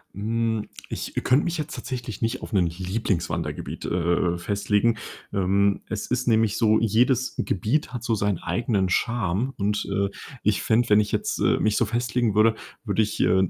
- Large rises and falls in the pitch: No, average, 2.9 semitones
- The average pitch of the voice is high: No, low, 110 Hz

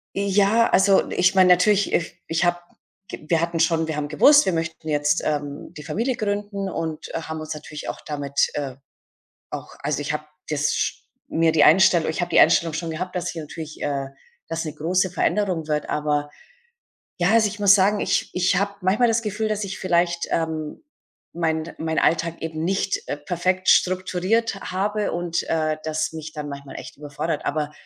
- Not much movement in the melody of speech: No, average, 3.7 semitones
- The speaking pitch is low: No, medium, 170 Hz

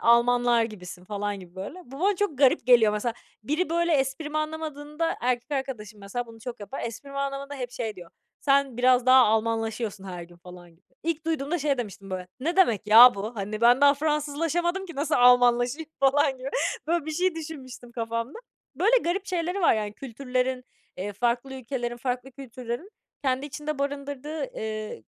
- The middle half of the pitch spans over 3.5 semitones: Yes, average, 4.7 semitones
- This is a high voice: Yes, very high, 255 Hz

